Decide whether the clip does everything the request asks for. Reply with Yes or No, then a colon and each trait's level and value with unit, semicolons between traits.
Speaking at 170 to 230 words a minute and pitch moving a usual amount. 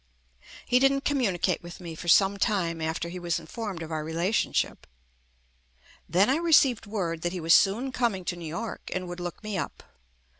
Yes: average, 190 wpm; average, 4.8 semitones